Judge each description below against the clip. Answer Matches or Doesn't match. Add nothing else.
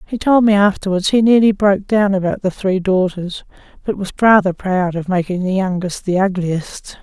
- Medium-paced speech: Matches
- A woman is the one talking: Matches